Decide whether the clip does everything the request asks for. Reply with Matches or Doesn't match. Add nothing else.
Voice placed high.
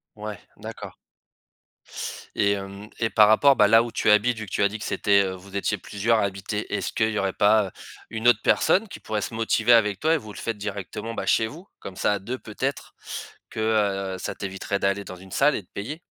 Doesn't match